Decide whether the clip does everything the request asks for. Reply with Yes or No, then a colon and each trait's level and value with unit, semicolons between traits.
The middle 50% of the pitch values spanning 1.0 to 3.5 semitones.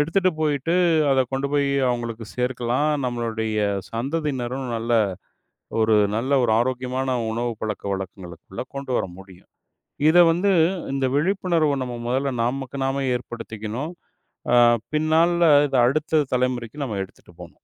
No: average, 4.0 semitones